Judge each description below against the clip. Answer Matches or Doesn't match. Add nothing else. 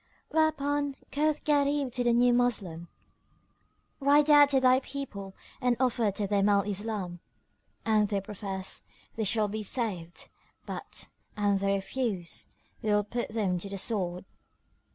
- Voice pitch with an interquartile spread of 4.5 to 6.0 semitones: Matches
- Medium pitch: Doesn't match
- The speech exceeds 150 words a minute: Doesn't match